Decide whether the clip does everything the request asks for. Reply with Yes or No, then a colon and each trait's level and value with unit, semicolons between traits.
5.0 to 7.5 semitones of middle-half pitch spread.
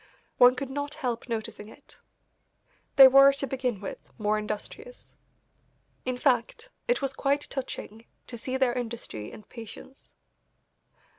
No: average, 3.3 semitones